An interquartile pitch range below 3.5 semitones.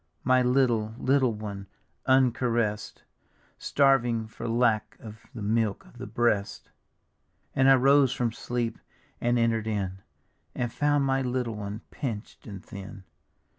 Yes: average, 3.0 semitones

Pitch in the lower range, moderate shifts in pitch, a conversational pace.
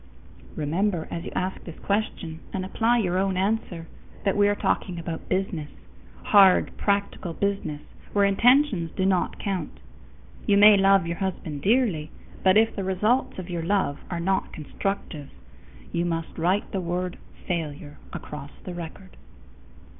No: medium, 185 Hz; average, 3.1 semitones; average, 155 wpm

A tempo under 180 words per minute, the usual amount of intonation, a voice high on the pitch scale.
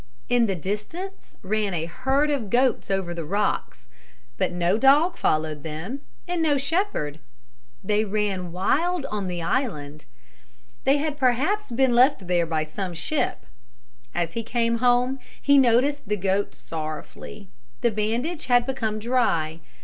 No: average, 145 wpm; wide, 7.2 semitones; high, 215 Hz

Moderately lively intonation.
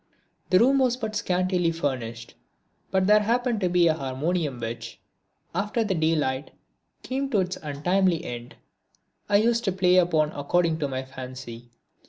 No: wide, 6.7 semitones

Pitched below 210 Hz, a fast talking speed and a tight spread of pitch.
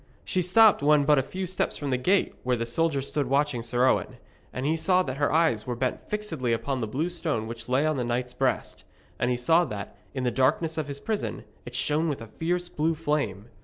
No: medium, 140 Hz; fast, 235 wpm; average, 4.8 semitones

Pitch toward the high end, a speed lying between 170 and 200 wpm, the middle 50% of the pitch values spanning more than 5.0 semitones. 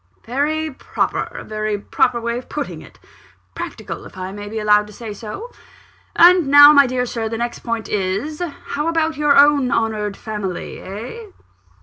Yes: high, 235 Hz; average, 175 wpm; wide, 5.6 semitones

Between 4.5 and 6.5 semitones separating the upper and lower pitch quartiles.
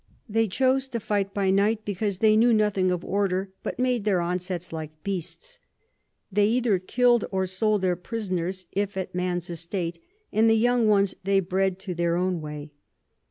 No: average, 3.2 semitones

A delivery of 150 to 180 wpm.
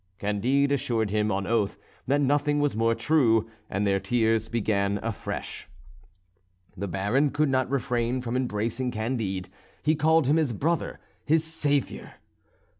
No: average, 140 wpm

